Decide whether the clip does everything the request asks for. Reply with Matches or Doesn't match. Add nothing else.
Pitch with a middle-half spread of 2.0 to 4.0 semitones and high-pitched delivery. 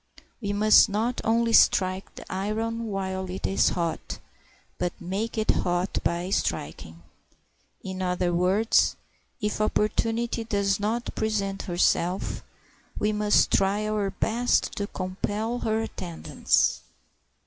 Matches